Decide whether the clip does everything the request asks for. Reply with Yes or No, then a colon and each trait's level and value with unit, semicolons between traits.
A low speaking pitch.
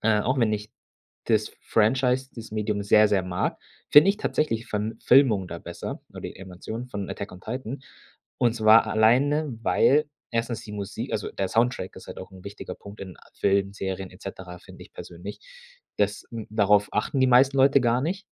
Yes: low, 110 Hz